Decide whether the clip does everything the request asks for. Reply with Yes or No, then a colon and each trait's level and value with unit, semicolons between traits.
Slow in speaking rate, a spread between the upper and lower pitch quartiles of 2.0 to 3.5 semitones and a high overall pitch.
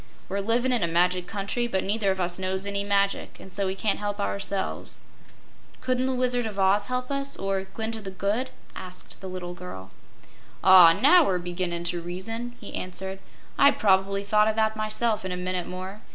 No: average, 195 wpm; average, 3.2 semitones; high, 195 Hz